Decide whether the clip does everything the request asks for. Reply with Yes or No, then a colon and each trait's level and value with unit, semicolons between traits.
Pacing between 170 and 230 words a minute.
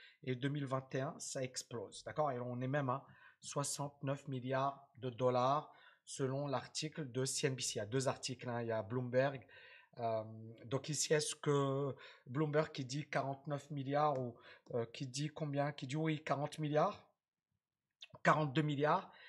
No: average, 155 wpm